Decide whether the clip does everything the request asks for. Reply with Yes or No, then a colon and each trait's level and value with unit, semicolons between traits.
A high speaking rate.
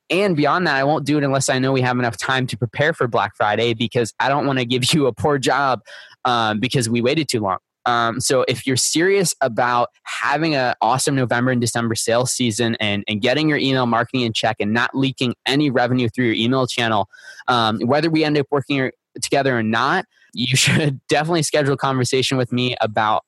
Yes: fast, 215 wpm